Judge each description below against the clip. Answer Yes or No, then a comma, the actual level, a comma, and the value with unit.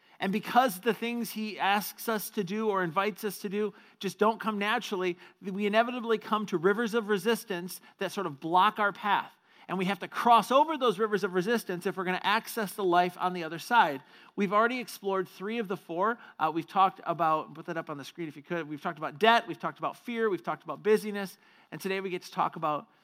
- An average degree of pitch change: Yes, average, 3.5 semitones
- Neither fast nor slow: No, fast, 235 wpm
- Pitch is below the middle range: No, high, 200 Hz